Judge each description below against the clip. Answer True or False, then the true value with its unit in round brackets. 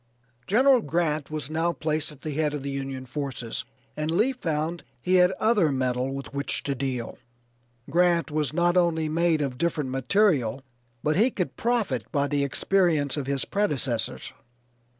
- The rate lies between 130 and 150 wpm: False (165 wpm)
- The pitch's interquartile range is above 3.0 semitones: True (4.1 semitones)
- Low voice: False (155 Hz)